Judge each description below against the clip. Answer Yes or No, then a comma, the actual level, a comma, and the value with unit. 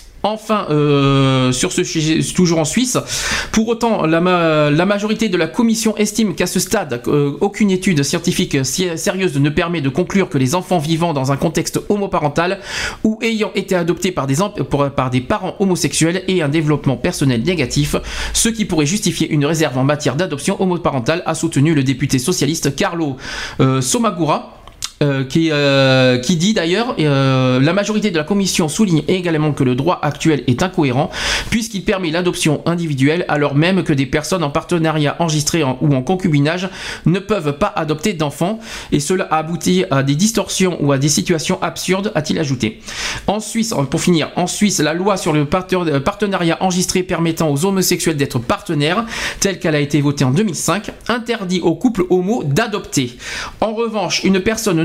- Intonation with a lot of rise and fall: No, average, 4.8 semitones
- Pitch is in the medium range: Yes, medium, 170 Hz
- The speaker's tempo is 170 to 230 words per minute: Yes, average, 175 wpm